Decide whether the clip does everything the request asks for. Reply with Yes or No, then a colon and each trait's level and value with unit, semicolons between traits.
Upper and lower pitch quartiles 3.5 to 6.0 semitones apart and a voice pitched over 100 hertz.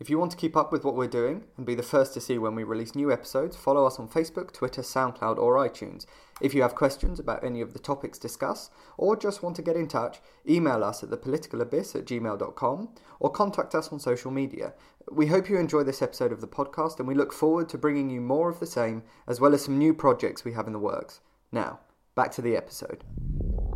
Yes: average, 4.4 semitones; medium, 140 Hz